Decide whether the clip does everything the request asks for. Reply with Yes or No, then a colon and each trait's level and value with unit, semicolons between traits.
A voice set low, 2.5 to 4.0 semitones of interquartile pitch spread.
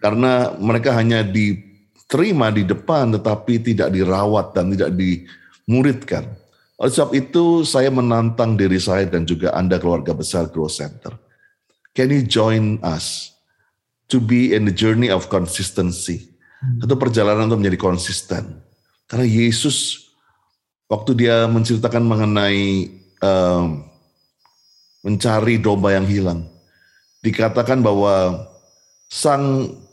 No: low, 105 Hz; average, 4.4 semitones